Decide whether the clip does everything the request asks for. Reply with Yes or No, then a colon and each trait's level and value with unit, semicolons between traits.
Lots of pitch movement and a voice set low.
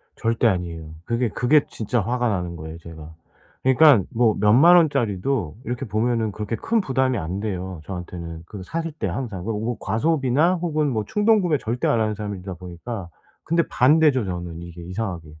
Yes: wide, 6.6 semitones; low, 110 Hz